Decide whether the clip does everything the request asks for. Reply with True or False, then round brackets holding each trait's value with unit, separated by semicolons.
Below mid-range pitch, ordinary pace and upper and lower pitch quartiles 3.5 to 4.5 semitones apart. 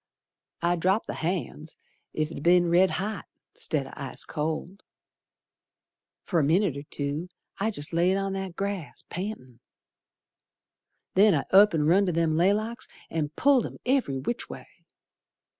False (175 Hz; 150 wpm; 4.2 semitones)